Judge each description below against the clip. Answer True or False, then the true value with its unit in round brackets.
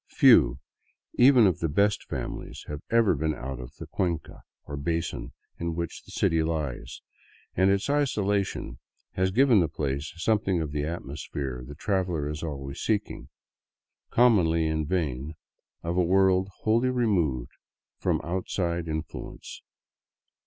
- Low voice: True (85 Hz)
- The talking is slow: False (150 wpm)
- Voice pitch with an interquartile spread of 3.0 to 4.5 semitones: False (4.9 semitones)